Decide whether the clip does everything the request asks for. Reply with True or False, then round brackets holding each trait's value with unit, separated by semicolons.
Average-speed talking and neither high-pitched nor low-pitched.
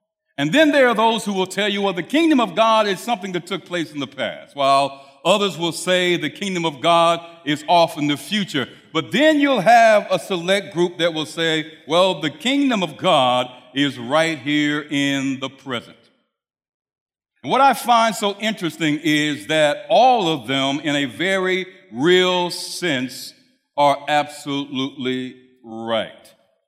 True (170 wpm; 170 Hz)